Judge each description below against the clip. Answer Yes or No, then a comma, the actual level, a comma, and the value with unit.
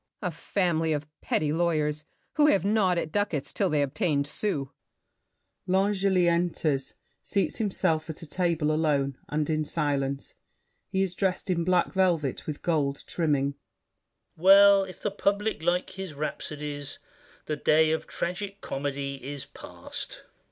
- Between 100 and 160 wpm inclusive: Yes, average, 145 wpm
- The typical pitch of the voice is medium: Yes, medium, 160 Hz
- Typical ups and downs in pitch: Yes, average, 4.3 semitones